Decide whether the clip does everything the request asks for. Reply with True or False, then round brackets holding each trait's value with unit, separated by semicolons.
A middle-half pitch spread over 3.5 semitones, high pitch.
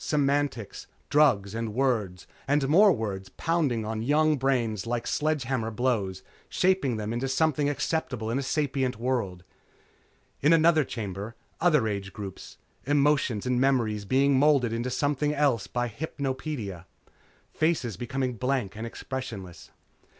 False (4.8 semitones; 130 Hz)